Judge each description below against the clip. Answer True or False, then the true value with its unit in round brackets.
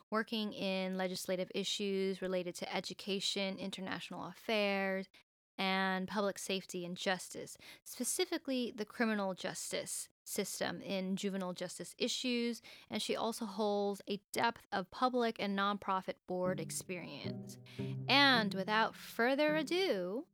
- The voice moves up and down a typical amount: True (3.1 semitones)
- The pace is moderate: False (115 wpm)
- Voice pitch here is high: True (195 Hz)